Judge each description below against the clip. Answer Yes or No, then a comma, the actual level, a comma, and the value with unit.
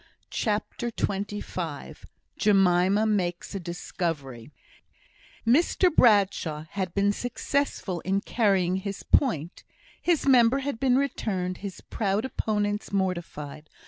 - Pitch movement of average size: Yes, average, 4.2 semitones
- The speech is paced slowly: Yes, slow, 105 wpm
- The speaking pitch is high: Yes, high, 200 Hz